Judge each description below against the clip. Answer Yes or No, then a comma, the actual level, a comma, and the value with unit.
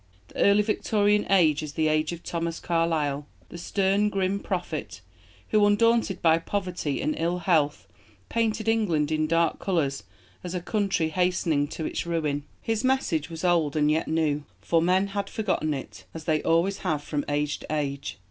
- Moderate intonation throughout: Yes, average, 4.4 semitones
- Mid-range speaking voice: Yes, medium, 170 Hz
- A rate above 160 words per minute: Yes, average, 175 wpm